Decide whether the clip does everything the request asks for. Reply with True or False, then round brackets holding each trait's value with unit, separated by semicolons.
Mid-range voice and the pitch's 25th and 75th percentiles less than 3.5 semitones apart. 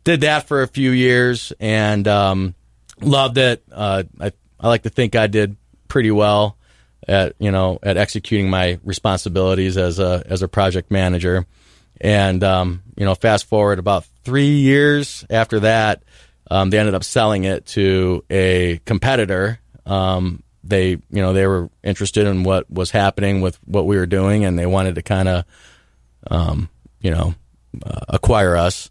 False (95 Hz; 2.8 semitones)